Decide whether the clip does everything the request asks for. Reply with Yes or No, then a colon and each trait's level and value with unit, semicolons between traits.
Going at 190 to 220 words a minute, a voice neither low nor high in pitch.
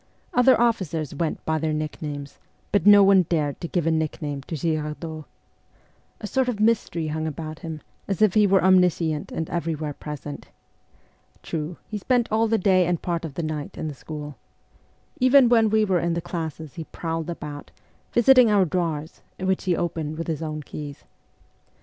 No: average, 180 wpm; medium, 165 Hz